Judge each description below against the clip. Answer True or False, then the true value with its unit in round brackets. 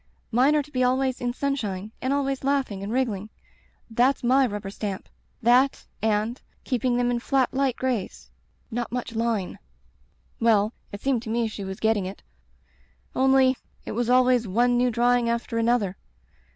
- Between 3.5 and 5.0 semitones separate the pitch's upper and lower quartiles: False (2.9 semitones)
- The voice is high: True (240 Hz)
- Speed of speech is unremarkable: True (180 wpm)